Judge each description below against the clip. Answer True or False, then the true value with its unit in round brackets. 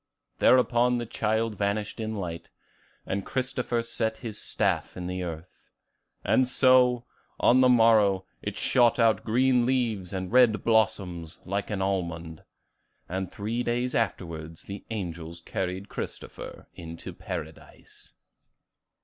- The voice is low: True (105 Hz)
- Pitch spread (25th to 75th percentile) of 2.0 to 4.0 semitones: False (4.5 semitones)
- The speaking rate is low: True (125 wpm)